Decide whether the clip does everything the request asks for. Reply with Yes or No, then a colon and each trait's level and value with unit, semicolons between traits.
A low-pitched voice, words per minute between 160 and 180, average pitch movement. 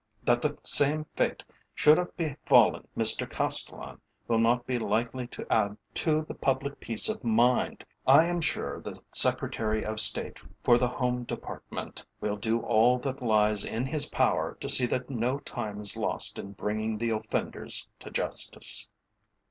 Yes: low, 120 Hz; average, 165 wpm; average, 3.9 semitones